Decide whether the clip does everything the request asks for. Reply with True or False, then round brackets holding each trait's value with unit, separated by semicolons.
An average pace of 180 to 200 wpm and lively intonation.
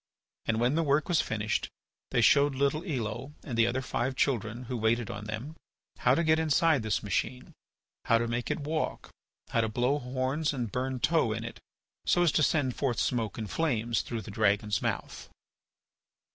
False (185 wpm; 4.2 semitones)